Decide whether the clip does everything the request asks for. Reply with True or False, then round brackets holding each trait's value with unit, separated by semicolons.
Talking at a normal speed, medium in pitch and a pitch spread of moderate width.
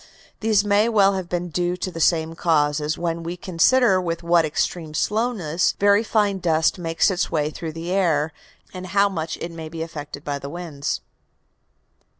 True (175 wpm; 170 Hz; 3.3 semitones)